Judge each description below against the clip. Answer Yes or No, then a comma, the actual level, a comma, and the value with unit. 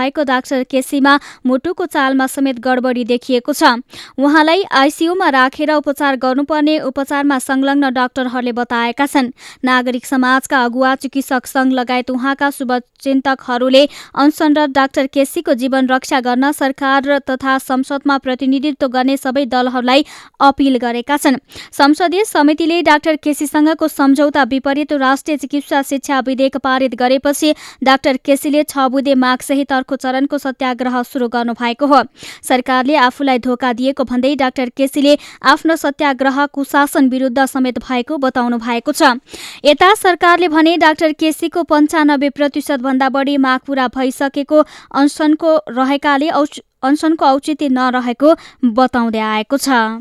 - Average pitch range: No, narrow, 2.1 semitones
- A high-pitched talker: Yes, very high, 275 Hz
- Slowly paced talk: Yes, slow, 125 wpm